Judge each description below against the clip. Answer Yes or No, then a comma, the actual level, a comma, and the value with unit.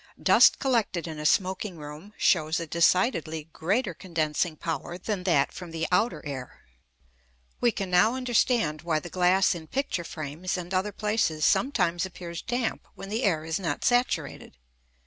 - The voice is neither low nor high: Yes, medium, 180 Hz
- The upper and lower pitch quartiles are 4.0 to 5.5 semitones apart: Yes, average, 4.5 semitones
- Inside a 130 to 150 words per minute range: No, average, 160 wpm